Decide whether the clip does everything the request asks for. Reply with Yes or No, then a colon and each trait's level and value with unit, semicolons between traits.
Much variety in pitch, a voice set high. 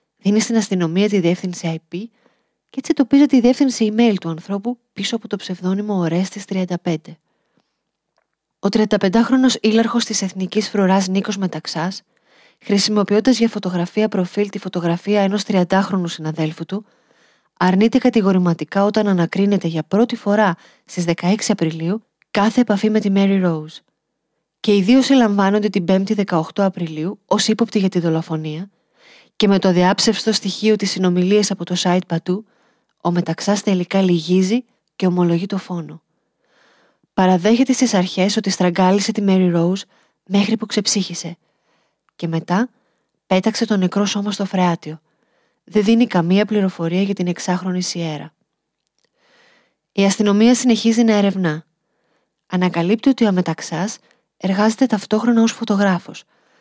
No: average, 3.4 semitones; high, 195 Hz